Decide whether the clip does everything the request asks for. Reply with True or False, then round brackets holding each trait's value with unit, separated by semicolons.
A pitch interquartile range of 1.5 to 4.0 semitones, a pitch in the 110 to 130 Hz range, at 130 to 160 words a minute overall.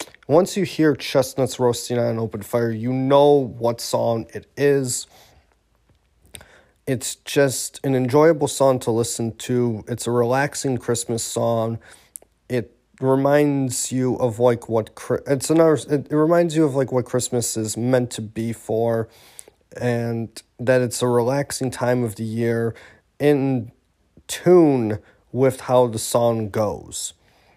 True (2.8 semitones; 125 Hz; 140 wpm)